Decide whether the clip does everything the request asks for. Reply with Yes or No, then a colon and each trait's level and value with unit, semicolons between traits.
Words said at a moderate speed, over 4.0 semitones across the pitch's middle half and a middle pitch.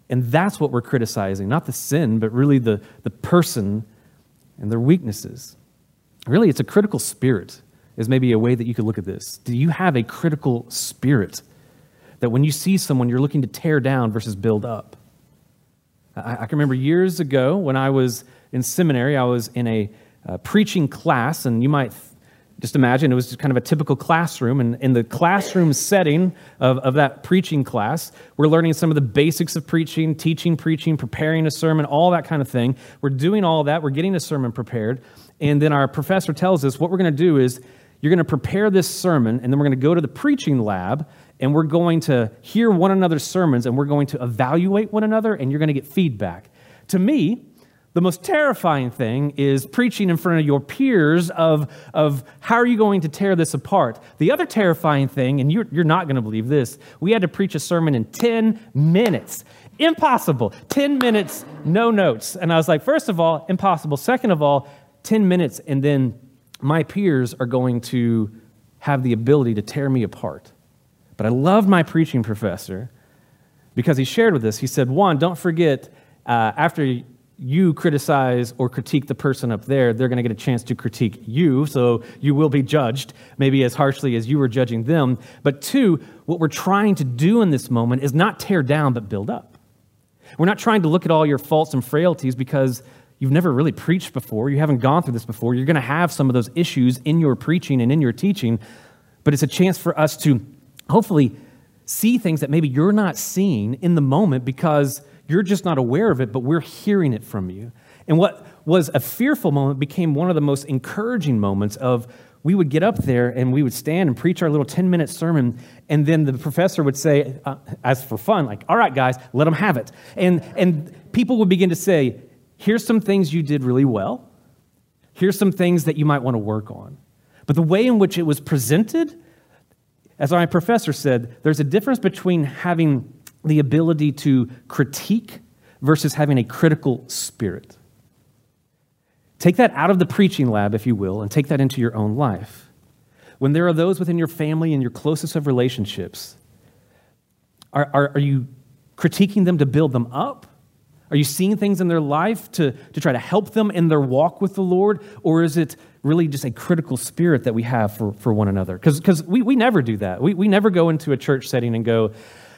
No: fast, 210 wpm; average, 5.2 semitones; medium, 145 Hz